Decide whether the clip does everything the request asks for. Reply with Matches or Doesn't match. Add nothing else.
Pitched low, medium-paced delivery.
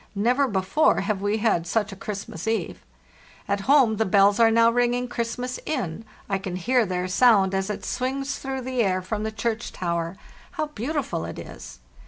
Doesn't match